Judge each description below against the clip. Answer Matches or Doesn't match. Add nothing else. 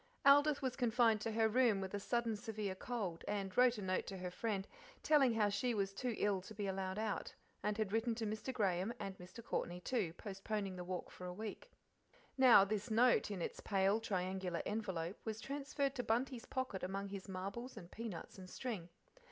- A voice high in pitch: Matches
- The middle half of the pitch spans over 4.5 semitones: Doesn't match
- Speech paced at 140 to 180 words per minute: Doesn't match